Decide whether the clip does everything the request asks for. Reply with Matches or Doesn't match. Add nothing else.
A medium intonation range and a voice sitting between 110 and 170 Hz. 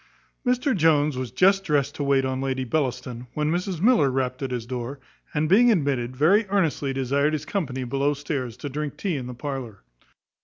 Matches